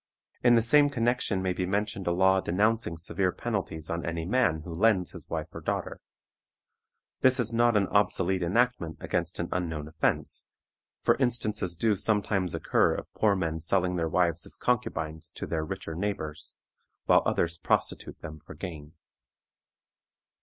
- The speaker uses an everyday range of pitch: Yes, average, 4.5 semitones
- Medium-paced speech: Yes, average, 160 wpm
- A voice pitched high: No, very low, 95 Hz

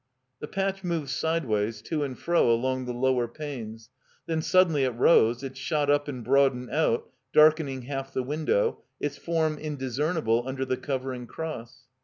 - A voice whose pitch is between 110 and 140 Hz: Yes, low, 135 Hz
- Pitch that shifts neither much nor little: Yes, average, 3.9 semitones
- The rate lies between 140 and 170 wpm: Yes, average, 160 wpm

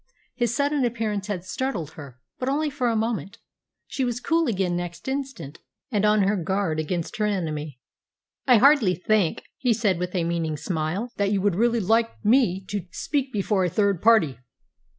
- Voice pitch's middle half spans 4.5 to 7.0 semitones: Yes, average, 5.2 semitones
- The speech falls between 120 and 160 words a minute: No, average, 180 wpm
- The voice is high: Yes, high, 205 Hz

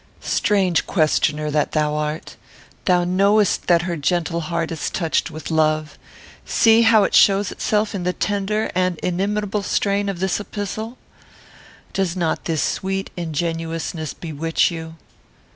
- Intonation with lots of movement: No, average, 3.7 semitones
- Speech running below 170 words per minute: Yes, average, 140 wpm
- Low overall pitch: No, medium, 175 Hz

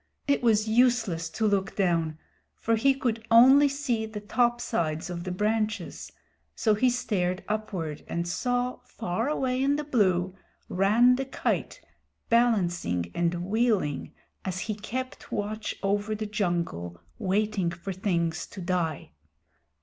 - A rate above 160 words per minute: No, slow, 135 wpm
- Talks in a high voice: Yes, high, 210 Hz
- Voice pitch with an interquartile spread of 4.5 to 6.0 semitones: Yes, average, 5.1 semitones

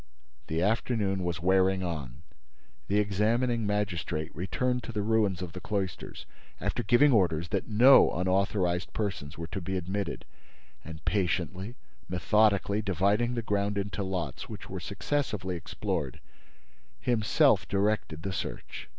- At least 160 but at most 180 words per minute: No, slow, 135 wpm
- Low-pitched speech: Yes, very low, 95 Hz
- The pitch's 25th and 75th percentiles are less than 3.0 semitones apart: No, average, 3.3 semitones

